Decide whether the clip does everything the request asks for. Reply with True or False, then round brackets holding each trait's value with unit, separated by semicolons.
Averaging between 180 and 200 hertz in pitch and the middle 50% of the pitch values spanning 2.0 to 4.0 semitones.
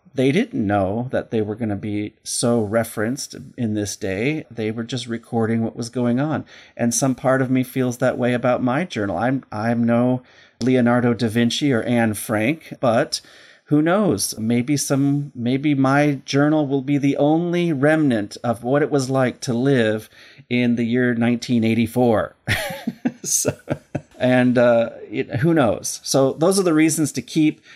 False (125 Hz; 3.2 semitones)